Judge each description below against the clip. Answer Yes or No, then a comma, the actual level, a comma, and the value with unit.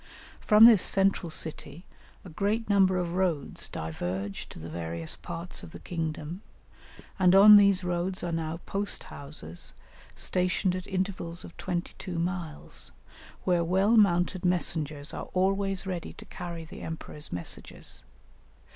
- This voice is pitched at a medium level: Yes, medium, 175 Hz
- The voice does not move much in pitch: No, average, 3.2 semitones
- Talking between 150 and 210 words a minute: No, average, 140 wpm